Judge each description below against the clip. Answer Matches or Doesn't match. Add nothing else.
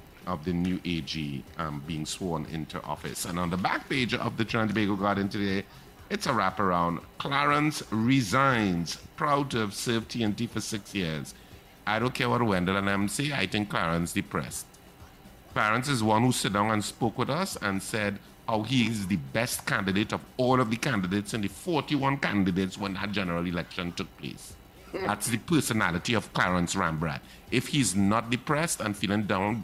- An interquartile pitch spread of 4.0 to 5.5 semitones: Matches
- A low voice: Matches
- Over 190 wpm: Doesn't match